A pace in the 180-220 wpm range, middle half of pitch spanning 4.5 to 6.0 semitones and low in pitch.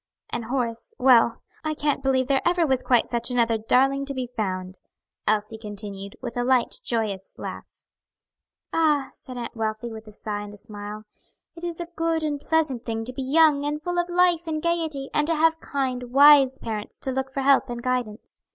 No: average, 200 wpm; average, 5.0 semitones; very high, 260 Hz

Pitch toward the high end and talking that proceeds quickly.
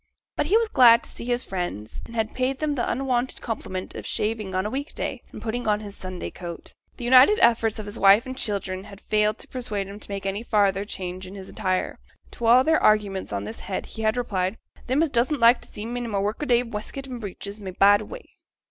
Yes: high, 215 Hz; fast, 240 wpm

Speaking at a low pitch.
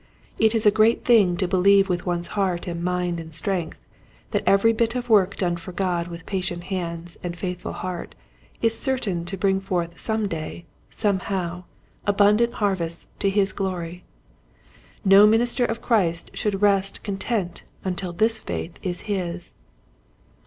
No: high, 190 Hz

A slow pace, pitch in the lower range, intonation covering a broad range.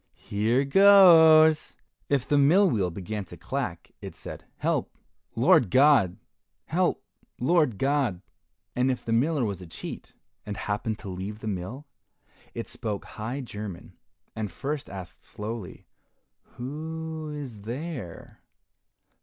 Yes: slow, 130 wpm; low, 120 Hz; wide, 6.5 semitones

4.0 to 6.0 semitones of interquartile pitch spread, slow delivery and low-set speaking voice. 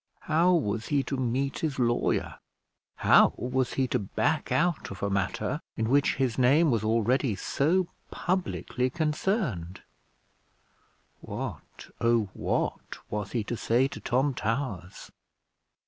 Yes: average, 4.5 semitones; slow, 130 wpm; low, 130 Hz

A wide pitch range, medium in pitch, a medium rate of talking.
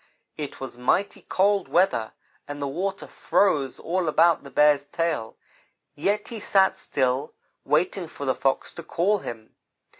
Yes: wide, 5.7 semitones; medium, 155 Hz; average, 150 wpm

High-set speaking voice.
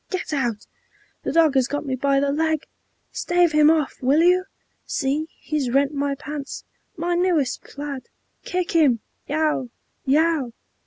Yes: very high, 295 Hz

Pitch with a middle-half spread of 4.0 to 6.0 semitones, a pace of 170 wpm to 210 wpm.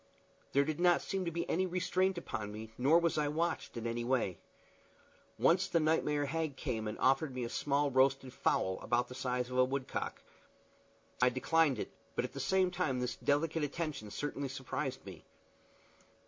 Yes: average, 4.5 semitones; average, 180 wpm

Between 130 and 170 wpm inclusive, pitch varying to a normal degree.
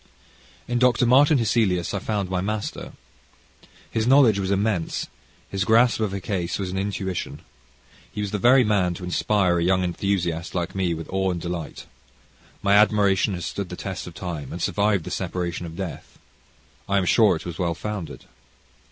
No: average, 180 wpm; average, 3.1 semitones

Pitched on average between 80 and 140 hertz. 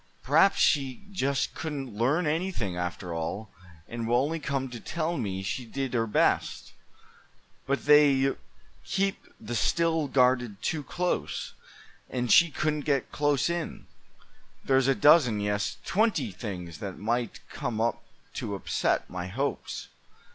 Yes: low, 135 Hz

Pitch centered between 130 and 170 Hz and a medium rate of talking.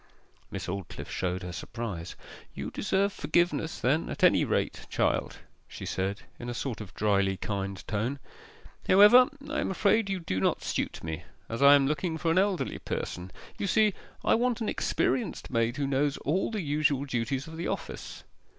Yes: medium, 140 Hz; average, 180 wpm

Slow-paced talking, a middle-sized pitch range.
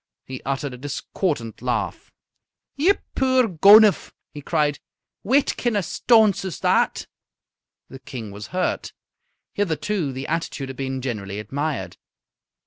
No: slow, 130 wpm; wide, 7.5 semitones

